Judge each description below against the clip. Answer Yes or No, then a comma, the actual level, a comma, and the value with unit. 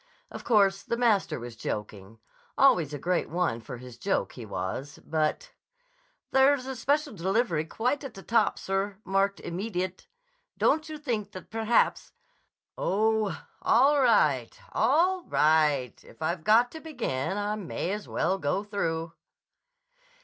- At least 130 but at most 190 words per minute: Yes, average, 140 wpm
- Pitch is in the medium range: No, high, 195 Hz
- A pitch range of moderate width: No, wide, 7.2 semitones